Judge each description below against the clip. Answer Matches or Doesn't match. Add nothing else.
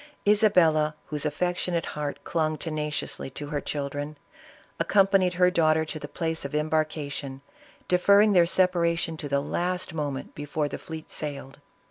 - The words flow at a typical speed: Matches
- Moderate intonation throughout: Matches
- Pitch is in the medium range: Matches